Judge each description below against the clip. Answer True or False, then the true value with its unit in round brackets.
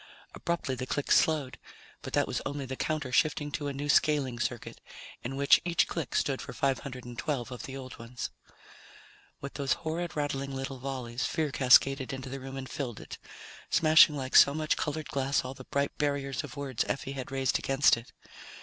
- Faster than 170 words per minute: True (185 wpm)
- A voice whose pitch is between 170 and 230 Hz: False (135 Hz)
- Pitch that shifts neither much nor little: False (1.9 semitones)